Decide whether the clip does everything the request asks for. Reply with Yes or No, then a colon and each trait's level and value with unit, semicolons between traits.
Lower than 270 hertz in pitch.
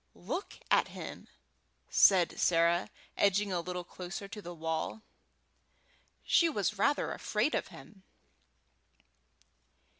Yes: medium, 185 Hz